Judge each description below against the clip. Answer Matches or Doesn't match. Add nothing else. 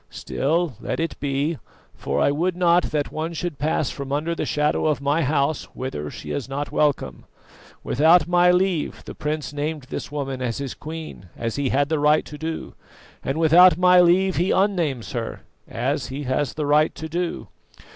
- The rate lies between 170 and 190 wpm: Matches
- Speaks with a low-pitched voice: Doesn't match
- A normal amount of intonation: Matches